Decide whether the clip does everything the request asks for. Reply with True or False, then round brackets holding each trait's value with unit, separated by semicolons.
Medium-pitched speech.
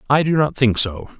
False (130 Hz)